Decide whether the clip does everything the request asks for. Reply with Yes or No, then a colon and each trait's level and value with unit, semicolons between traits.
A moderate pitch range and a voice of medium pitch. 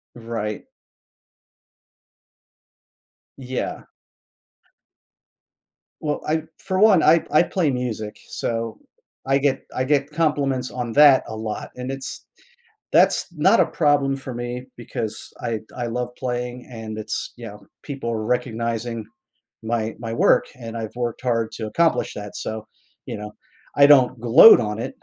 No: average, 3.3 semitones; low, 120 Hz